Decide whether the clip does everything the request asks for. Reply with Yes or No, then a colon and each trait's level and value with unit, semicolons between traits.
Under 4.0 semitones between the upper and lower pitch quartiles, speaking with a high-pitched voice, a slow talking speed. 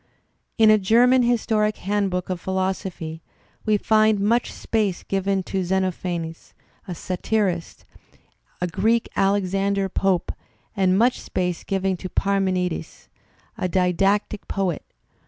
Yes: narrow, 2.4 semitones; high, 195 Hz; slow, 120 wpm